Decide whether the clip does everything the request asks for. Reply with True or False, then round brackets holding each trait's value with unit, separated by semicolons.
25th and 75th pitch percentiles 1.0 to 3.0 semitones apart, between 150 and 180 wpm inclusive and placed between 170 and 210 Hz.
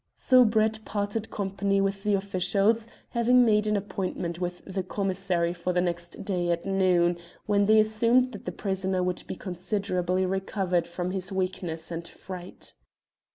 True (2.6 semitones; 155 wpm; 190 Hz)